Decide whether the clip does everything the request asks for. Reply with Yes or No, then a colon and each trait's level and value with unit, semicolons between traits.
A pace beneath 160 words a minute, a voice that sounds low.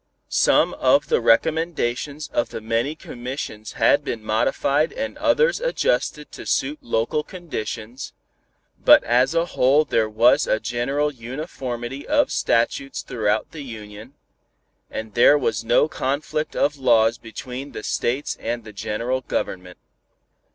Yes: slow, 135 wpm; low, 125 Hz